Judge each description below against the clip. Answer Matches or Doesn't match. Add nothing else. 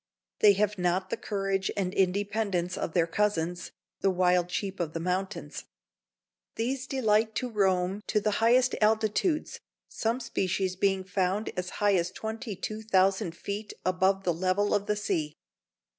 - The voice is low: Doesn't match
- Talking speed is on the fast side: Doesn't match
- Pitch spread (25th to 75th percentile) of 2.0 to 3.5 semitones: Matches